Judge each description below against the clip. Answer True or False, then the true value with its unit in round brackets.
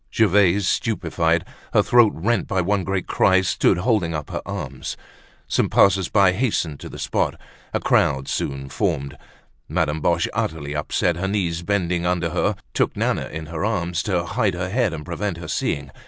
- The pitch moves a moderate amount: True (3.4 semitones)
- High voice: False (90 Hz)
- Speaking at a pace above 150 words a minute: True (175 wpm)